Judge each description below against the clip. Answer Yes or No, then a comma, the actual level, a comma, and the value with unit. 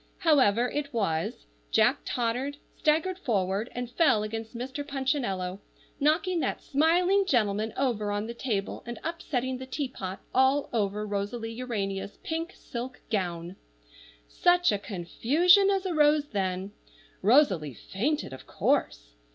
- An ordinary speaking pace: No, slow, 125 wpm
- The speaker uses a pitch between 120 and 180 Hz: No, high, 240 Hz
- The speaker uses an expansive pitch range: Yes, wide, 6.6 semitones